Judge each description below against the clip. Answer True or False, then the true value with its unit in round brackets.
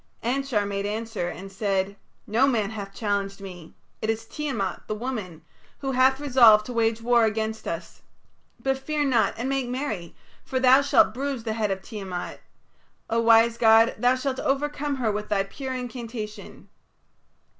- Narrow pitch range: False (4.0 semitones)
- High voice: True (225 Hz)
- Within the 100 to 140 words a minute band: False (165 wpm)